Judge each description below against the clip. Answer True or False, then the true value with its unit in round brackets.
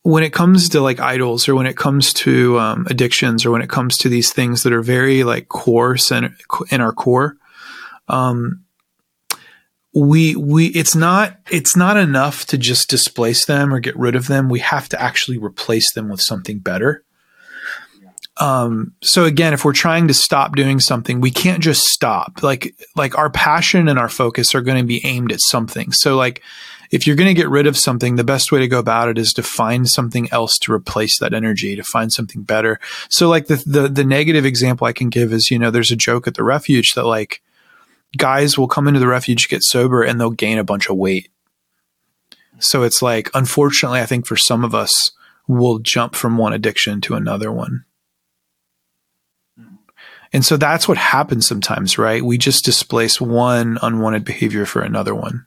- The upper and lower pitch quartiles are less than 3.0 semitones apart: False (3.6 semitones)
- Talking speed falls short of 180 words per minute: False (200 wpm)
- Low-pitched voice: True (125 Hz)